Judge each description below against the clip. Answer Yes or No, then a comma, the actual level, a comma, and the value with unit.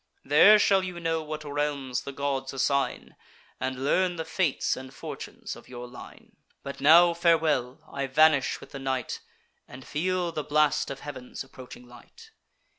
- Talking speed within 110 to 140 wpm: No, average, 160 wpm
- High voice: No, medium, 145 Hz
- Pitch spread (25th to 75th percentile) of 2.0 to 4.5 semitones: Yes, average, 3.7 semitones